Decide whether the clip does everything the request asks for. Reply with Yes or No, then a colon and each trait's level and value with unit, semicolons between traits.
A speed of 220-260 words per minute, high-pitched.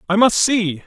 No: fast, 210 wpm; high, 205 Hz